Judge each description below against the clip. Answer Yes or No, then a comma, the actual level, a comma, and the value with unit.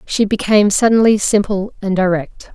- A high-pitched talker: Yes, high, 200 Hz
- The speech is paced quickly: No, average, 140 wpm